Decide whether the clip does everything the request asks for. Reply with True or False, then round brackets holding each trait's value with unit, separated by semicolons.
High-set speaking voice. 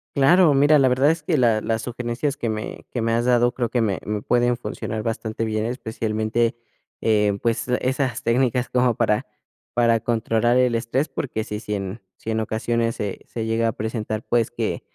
False (115 Hz)